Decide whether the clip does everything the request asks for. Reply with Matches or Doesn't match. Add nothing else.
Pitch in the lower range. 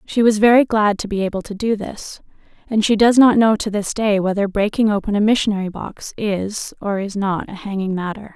Doesn't match